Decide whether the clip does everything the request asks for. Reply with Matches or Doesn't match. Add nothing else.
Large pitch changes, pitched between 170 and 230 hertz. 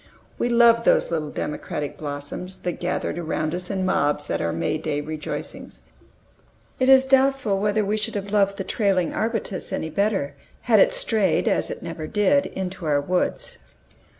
Matches